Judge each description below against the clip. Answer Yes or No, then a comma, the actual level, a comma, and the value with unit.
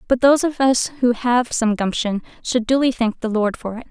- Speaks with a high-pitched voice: Yes, high, 240 Hz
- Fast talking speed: Yes, fast, 230 wpm